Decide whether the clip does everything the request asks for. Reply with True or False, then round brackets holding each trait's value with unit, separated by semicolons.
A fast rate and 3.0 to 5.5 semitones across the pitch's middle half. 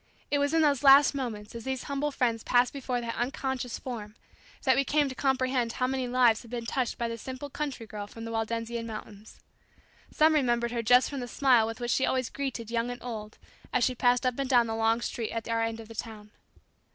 False (230 wpm; 2.6 semitones)